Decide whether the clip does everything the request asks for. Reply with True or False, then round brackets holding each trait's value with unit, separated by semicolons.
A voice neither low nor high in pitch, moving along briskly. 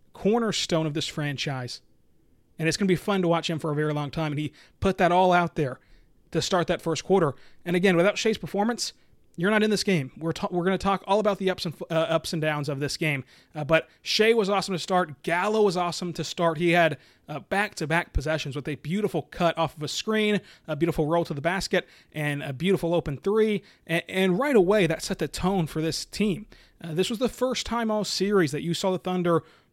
True (170 Hz; 240 wpm)